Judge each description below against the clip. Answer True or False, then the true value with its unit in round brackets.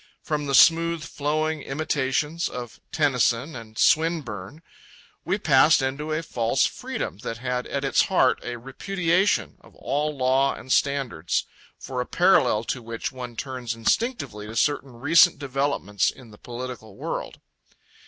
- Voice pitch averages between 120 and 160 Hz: True (135 Hz)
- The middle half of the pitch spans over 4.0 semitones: True (4.4 semitones)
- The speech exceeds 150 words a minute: False (145 wpm)